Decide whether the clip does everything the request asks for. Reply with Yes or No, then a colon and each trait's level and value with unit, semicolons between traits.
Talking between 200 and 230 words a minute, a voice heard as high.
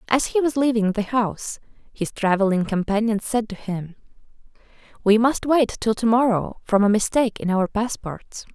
No: average, 170 wpm; high, 220 Hz